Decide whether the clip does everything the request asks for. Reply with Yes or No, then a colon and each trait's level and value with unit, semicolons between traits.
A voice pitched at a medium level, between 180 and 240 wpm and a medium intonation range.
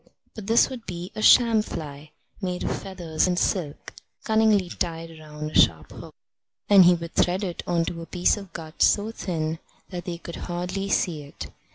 Yes: medium, 175 Hz; average, 190 wpm; average, 3.2 semitones